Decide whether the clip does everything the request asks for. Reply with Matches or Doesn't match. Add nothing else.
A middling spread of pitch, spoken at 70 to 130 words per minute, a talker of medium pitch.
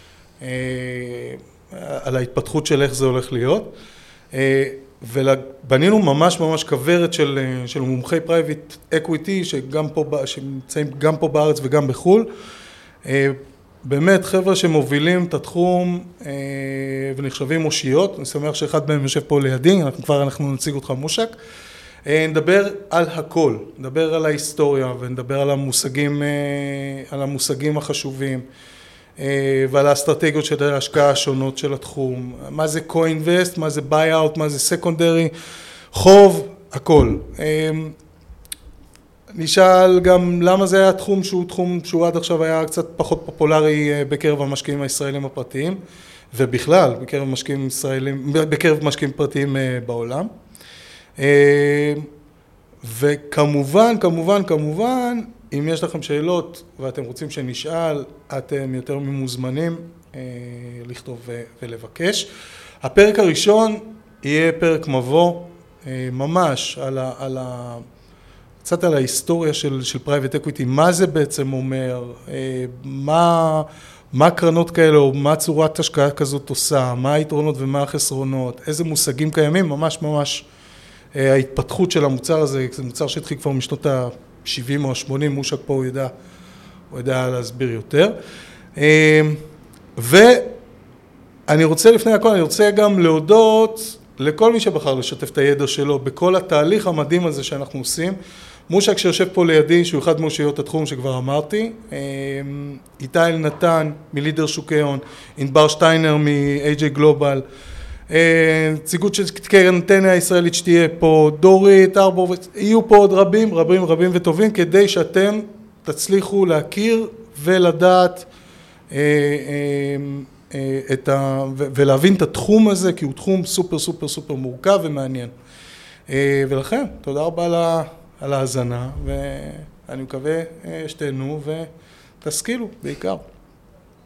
Matches